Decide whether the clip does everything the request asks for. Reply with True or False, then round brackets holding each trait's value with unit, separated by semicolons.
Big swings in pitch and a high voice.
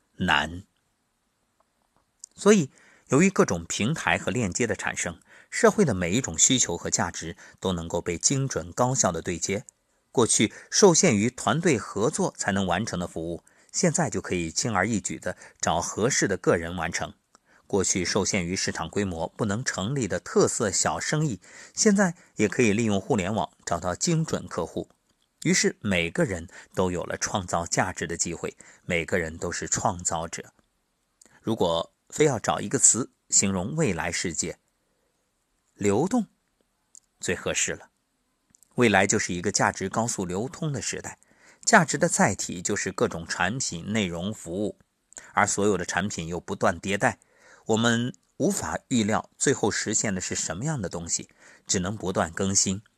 False (7.3 semitones; 100 Hz)